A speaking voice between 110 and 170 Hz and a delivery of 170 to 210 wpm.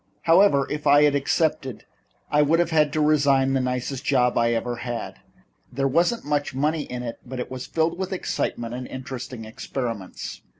Yes: low, 135 Hz; average, 180 wpm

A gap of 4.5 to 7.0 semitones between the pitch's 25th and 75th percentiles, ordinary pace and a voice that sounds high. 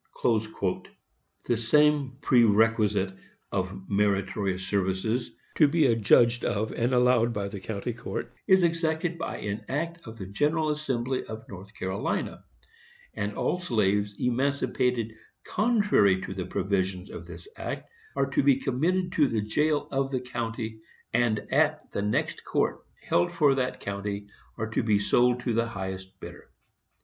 No: average, 5.3 semitones; average, 150 wpm; low, 115 Hz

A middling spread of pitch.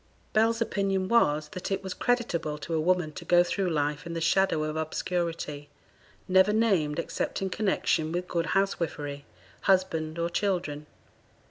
Yes: average, 3.7 semitones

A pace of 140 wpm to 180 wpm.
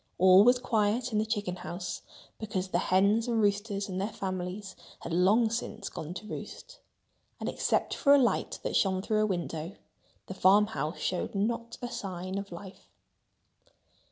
Yes: average, 165 wpm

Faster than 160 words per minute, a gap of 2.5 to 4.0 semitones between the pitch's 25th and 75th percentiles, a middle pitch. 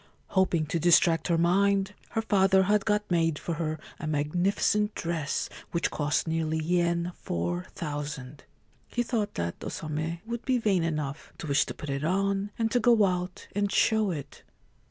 No: average, 170 wpm; average, 4.5 semitones; medium, 170 Hz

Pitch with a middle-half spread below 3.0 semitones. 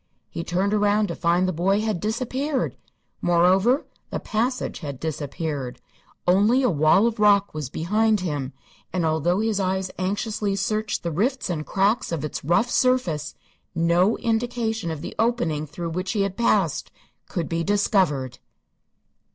No: average, 4.7 semitones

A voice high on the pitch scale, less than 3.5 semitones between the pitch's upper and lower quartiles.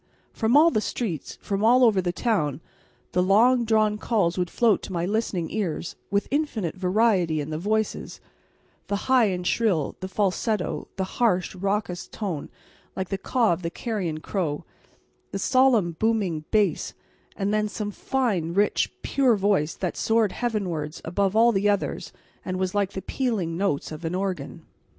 No: high, 200 Hz; average, 3.8 semitones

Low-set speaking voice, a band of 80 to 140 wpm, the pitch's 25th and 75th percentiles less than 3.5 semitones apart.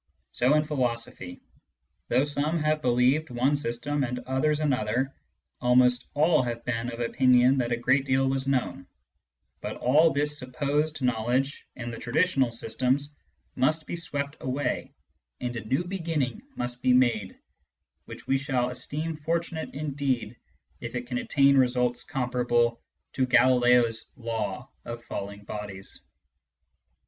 Yes: low, 130 Hz; slow, 135 wpm; average, 2.9 semitones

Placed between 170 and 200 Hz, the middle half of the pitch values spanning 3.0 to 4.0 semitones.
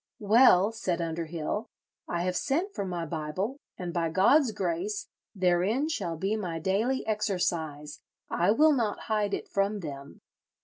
No: high, 190 Hz; average, 4.4 semitones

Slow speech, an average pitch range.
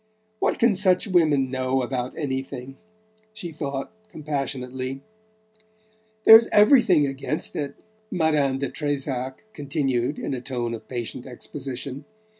Yes: slow, 115 wpm; average, 3.1 semitones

